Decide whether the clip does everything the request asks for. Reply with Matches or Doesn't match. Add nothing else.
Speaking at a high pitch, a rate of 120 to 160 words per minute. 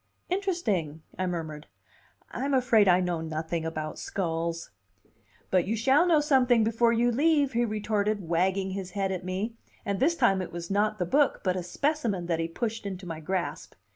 Doesn't match